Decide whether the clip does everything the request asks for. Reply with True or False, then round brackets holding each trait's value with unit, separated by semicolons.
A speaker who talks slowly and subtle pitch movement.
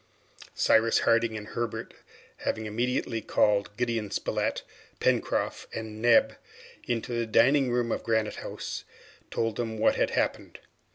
True (130 wpm; 1.3 semitones)